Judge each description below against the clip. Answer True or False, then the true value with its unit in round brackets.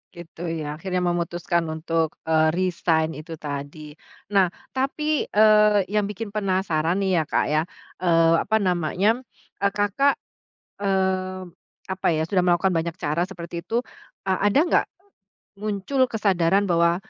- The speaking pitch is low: False (180 Hz)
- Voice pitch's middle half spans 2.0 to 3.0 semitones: False (3.4 semitones)